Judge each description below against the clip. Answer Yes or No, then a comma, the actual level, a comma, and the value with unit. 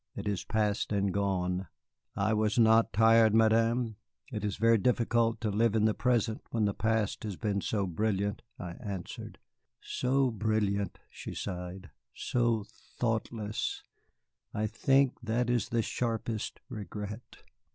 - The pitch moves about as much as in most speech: No, narrow, 2.1 semitones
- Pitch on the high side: No, low, 110 Hz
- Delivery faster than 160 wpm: No, average, 140 wpm